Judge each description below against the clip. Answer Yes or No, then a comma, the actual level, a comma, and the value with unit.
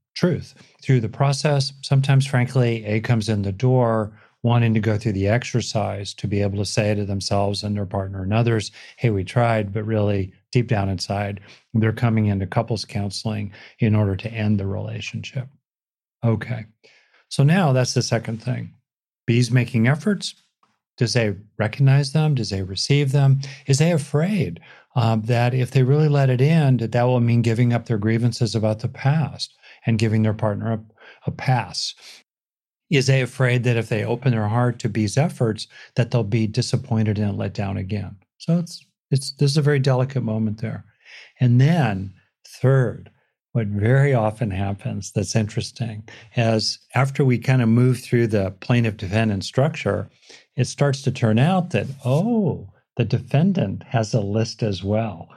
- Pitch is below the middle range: Yes, low, 115 Hz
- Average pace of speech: Yes, average, 170 wpm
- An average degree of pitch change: Yes, average, 3.5 semitones